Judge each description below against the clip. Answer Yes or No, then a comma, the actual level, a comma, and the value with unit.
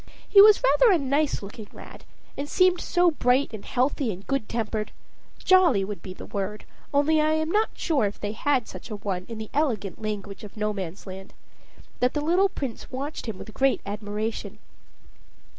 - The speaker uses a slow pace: No, average, 180 wpm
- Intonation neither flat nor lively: No, wide, 6.7 semitones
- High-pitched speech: Yes, high, 235 Hz